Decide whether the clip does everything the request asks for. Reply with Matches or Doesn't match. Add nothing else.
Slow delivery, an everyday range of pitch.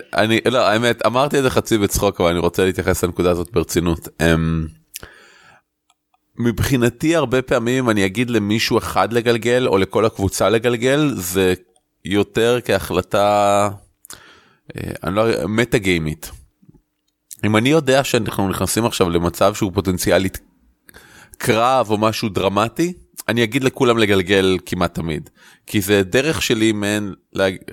Doesn't match